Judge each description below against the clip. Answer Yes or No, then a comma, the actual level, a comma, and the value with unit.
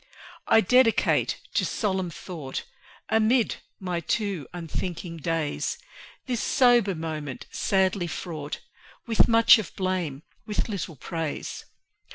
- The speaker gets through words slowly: Yes, slow, 110 wpm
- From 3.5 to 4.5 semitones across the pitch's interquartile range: No, average, 5.0 semitones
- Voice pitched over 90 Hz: Yes, medium, 185 Hz